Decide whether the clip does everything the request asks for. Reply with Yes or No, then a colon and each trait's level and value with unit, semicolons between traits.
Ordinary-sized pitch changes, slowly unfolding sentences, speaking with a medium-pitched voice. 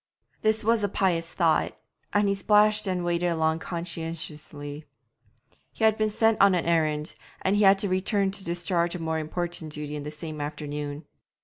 No: average, 4.2 semitones; average, 175 wpm; medium, 170 Hz